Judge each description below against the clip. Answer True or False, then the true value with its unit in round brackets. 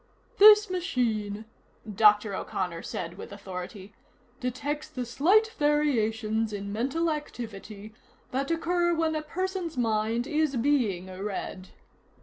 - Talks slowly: True (115 wpm)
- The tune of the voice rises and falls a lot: True (6.9 semitones)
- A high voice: True (240 Hz)